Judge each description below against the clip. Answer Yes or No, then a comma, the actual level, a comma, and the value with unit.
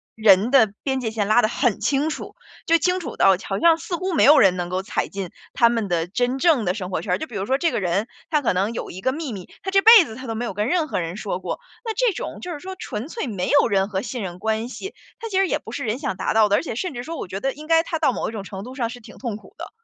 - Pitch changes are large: Yes, wide, 7.6 semitones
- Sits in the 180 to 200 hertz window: No, high, 235 Hz